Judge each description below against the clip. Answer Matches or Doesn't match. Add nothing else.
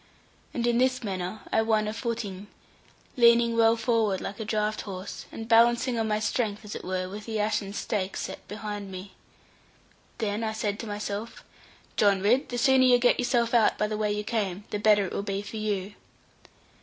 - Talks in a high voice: Matches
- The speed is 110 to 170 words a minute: Doesn't match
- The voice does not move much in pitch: Matches